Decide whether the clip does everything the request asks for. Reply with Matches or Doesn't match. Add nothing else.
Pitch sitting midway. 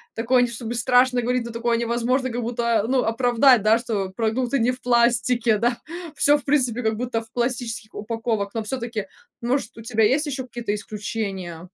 Doesn't match